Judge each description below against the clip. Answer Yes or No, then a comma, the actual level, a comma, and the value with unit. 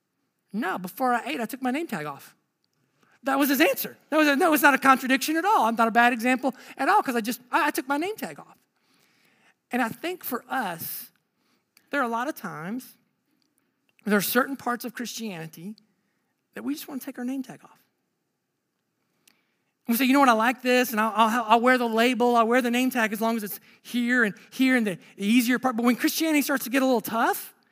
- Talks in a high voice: Yes, very high, 250 Hz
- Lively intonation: No, average, 3.3 semitones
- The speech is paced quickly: Yes, fast, 235 wpm